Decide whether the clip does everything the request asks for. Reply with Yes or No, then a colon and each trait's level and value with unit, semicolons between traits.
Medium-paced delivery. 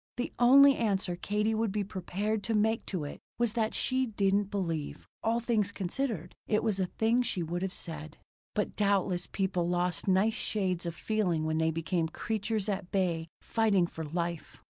Yes: average, 180 wpm